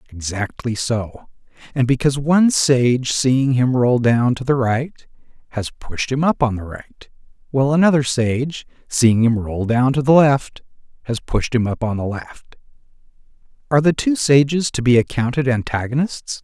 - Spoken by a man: Yes, male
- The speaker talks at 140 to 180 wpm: Yes, average, 165 wpm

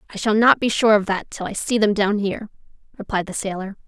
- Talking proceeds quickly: Yes, fast, 250 wpm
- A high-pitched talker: Yes, high, 210 Hz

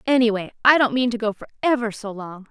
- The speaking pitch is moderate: No, high, 230 Hz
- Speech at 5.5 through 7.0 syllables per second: Yes, 6.1 syllables/s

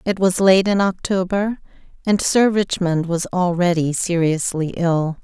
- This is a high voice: No, medium, 180 Hz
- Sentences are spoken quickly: No, slow, 135 wpm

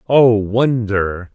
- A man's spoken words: Yes, male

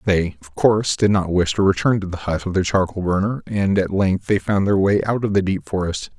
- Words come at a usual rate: No, fast, 260 wpm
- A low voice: Yes, very low, 95 Hz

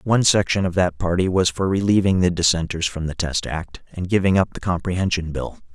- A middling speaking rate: No, fast, 210 wpm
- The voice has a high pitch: No, very low, 90 Hz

